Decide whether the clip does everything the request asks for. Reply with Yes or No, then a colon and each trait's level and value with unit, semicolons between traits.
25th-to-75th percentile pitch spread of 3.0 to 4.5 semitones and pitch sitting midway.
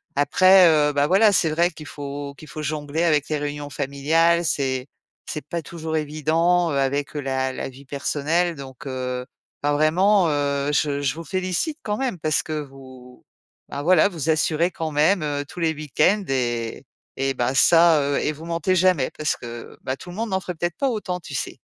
Yes: average, 3.5 semitones; medium, 150 Hz